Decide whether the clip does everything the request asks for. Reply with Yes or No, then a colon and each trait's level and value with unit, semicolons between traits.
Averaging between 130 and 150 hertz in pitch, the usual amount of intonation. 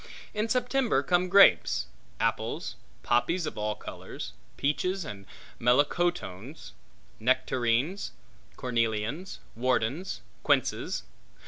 No: low, 135 Hz; wide, 8.0 semitones